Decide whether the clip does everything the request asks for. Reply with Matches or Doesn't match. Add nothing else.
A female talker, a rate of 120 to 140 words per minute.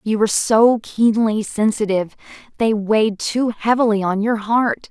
Matches